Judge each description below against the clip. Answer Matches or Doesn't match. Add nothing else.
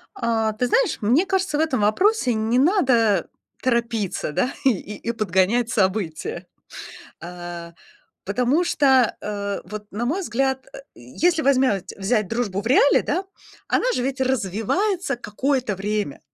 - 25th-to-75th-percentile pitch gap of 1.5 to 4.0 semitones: Doesn't match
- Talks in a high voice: Matches